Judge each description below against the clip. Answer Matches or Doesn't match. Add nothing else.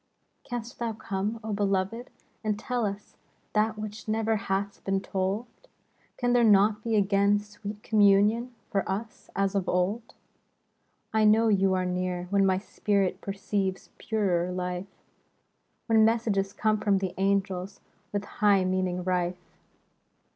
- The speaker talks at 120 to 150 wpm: Matches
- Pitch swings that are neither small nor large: Doesn't match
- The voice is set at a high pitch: Matches